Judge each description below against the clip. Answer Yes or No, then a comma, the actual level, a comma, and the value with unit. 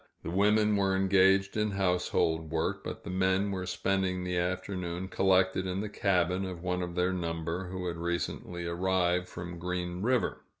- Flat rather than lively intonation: Yes, narrow, 1.5 semitones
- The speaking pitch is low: Yes, very low, 90 Hz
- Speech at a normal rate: Yes, average, 170 wpm